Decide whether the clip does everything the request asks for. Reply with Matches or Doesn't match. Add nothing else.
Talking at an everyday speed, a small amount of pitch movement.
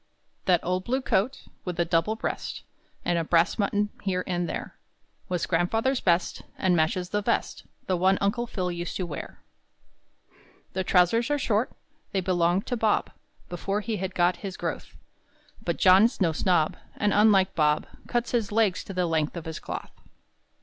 Doesn't match